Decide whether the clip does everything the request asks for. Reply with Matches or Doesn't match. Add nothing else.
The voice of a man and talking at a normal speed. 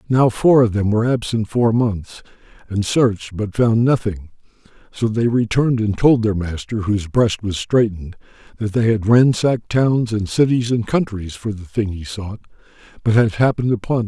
Matches